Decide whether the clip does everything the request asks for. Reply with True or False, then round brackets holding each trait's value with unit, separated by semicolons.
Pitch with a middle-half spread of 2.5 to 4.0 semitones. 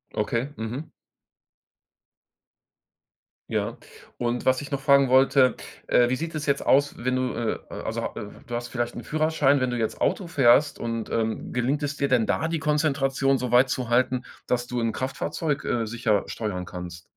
True (2.9 semitones)